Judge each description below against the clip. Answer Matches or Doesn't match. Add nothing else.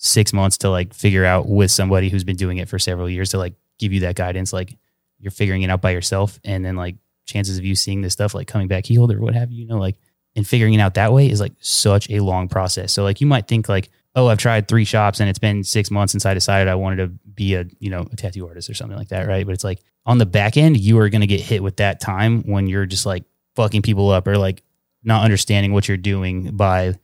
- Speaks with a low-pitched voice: Matches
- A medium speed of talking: Doesn't match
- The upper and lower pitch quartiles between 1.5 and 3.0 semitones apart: Matches